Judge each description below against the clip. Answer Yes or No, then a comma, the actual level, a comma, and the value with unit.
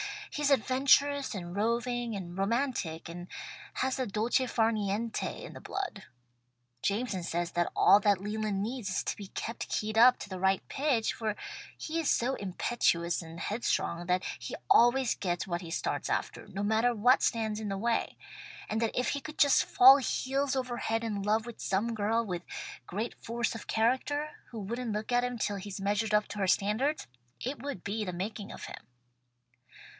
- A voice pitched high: Yes, high, 220 Hz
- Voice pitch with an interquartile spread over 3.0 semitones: Yes, average, 3.8 semitones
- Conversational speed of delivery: Yes, average, 190 wpm